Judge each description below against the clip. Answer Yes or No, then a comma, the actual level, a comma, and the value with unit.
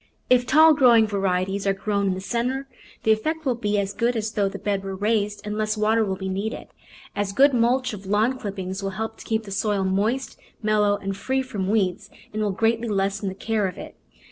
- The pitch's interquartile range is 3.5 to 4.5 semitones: No, average, 2.8 semitones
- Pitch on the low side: No, high, 210 Hz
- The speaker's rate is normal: No, fast, 220 wpm